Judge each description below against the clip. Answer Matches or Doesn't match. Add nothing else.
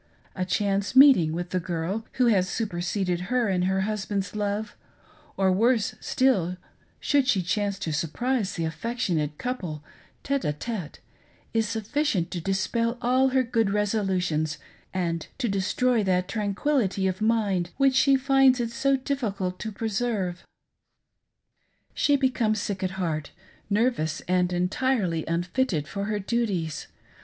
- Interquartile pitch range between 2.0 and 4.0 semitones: Doesn't match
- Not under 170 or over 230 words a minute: Doesn't match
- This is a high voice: Matches